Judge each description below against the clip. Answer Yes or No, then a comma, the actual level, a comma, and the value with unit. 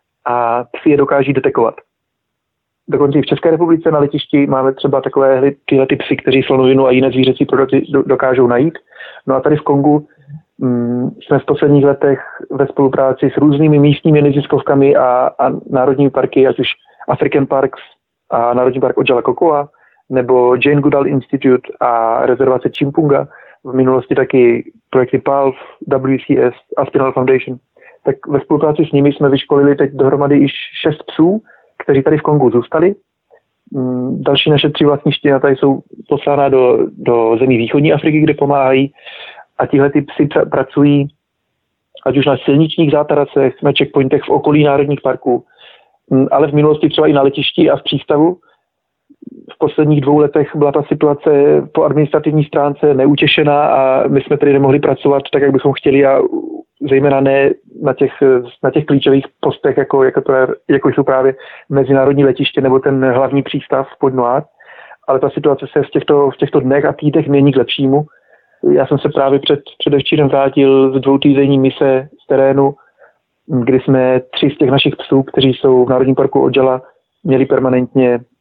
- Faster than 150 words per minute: Yes, fast, 165 wpm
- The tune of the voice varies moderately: No, narrow, 1.8 semitones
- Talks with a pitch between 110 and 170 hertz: Yes, medium, 140 Hz